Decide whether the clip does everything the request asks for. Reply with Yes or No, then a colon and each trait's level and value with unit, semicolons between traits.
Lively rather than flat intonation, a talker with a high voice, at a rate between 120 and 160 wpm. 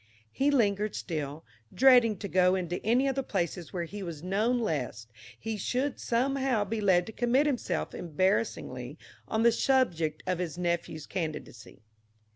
Yes: wide, 5.8 semitones; high, 195 Hz; average, 155 wpm